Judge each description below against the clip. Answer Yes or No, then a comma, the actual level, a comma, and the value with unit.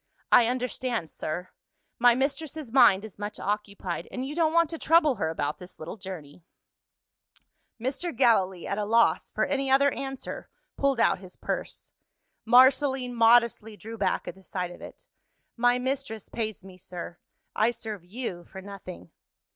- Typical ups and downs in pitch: No, wide, 5.7 semitones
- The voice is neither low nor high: No, high, 225 Hz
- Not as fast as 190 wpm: Yes, average, 160 wpm